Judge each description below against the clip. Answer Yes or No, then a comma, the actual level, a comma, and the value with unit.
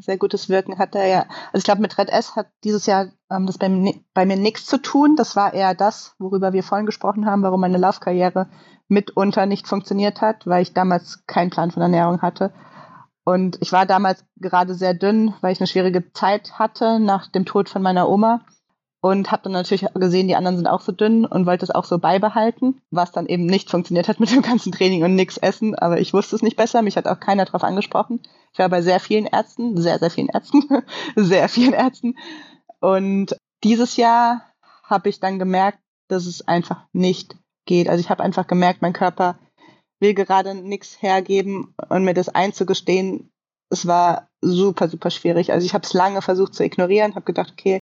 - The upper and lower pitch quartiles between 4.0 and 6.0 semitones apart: No, narrow, 2.5 semitones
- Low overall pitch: No, high, 190 Hz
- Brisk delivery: Yes, fast, 205 wpm